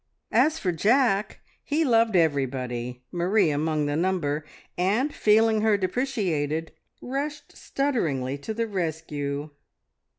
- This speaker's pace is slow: Yes, slow, 110 wpm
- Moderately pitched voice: Yes, medium, 180 Hz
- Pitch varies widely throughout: Yes, wide, 7.4 semitones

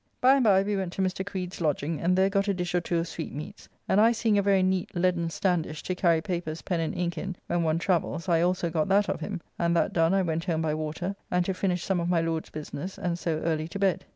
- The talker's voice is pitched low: No, medium, 175 Hz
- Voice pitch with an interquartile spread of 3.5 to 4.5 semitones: No, narrow, 2.6 semitones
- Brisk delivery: Yes, fast, 265 wpm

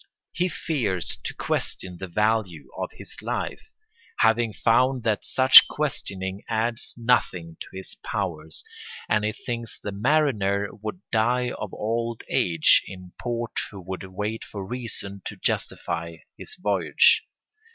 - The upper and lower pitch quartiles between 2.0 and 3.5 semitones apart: No, average, 4.1 semitones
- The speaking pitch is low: Yes, low, 110 Hz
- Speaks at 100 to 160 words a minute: Yes, slow, 135 wpm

